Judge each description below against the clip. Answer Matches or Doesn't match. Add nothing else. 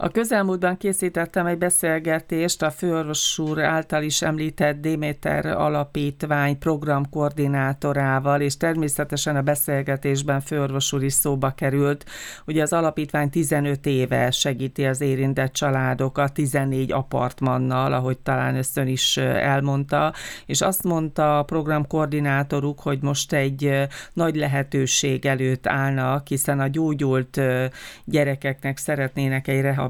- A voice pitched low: Doesn't match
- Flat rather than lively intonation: Matches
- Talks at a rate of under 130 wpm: Matches